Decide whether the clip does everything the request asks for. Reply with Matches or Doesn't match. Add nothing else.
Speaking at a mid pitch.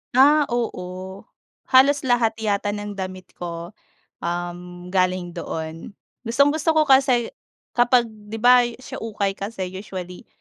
Doesn't match